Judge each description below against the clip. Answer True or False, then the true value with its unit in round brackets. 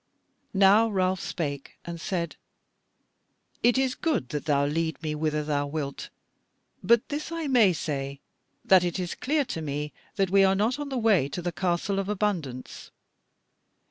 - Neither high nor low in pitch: True (180 Hz)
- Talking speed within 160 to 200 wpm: True (165 wpm)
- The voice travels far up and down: True (6.0 semitones)